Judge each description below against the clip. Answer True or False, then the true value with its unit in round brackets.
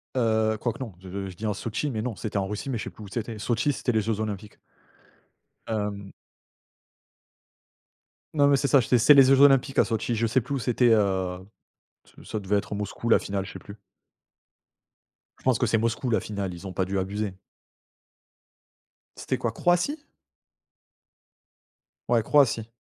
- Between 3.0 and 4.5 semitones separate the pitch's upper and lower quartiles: True (3.6 semitones)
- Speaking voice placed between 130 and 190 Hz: False (110 Hz)